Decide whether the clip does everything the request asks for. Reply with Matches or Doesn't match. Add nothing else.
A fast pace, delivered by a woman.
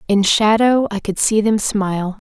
Doesn't match